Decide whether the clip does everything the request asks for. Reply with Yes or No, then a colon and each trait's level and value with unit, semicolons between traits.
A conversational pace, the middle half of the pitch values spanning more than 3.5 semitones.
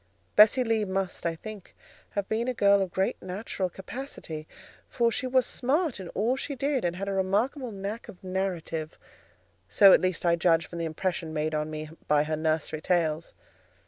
Yes: average, 185 wpm; average, 5.1 semitones